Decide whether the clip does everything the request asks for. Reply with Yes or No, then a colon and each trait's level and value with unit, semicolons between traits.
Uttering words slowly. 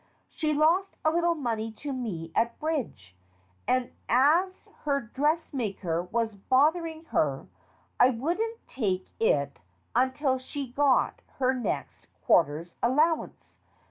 Yes: slow, 115 wpm